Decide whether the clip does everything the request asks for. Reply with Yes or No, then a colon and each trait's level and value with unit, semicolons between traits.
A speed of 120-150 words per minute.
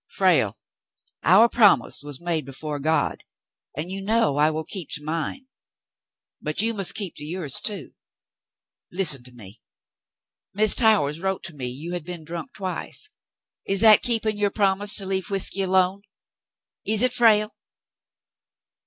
Yes: average, 145 wpm